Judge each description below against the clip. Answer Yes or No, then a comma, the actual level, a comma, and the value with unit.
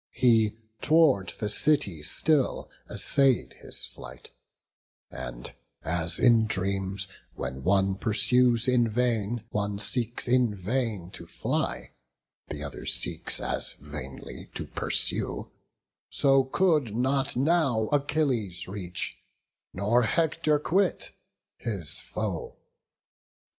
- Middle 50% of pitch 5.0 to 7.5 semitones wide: Yes, wide, 5.5 semitones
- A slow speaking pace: Yes, slow, 105 wpm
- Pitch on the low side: Yes, low, 115 Hz